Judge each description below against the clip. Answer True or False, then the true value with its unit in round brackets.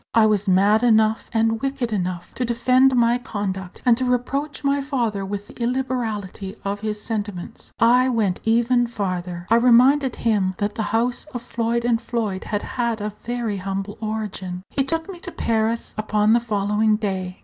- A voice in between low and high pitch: False (225 Hz)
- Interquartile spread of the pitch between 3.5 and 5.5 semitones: False (3.0 semitones)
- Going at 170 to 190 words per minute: True (175 wpm)